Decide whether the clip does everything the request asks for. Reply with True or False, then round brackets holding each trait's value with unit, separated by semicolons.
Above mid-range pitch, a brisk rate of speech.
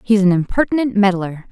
False (205 Hz; 160 wpm)